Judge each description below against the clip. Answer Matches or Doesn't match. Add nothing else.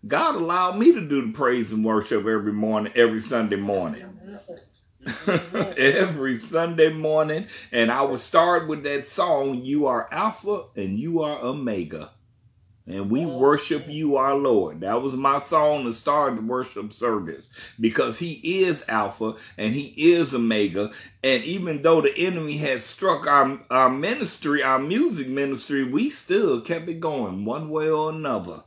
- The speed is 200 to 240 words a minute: Doesn't match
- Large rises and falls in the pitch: Matches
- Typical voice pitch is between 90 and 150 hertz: Matches